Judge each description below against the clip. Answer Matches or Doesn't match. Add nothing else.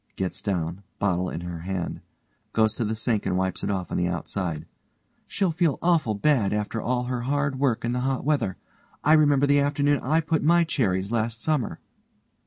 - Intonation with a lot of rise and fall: Matches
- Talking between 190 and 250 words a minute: Matches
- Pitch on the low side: Matches